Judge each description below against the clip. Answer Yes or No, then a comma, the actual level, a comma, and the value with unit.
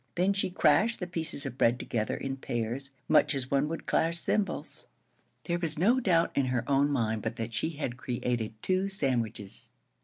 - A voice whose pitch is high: No, medium, 140 Hz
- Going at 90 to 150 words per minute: No, average, 185 wpm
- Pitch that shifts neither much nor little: No, wide, 6.2 semitones